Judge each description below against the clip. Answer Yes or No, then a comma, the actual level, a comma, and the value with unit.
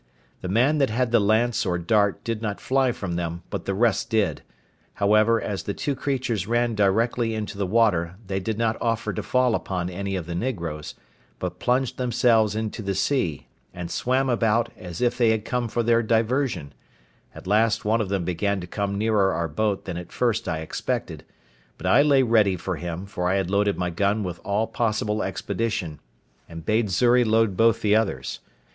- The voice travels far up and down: No, average, 3.6 semitones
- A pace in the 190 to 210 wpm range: Yes, average, 195 wpm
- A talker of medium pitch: No, low, 105 Hz